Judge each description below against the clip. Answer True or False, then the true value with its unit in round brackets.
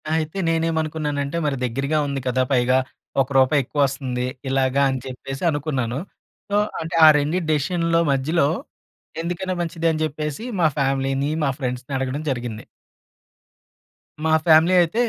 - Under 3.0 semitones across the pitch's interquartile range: False (3.3 semitones)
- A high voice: False (145 Hz)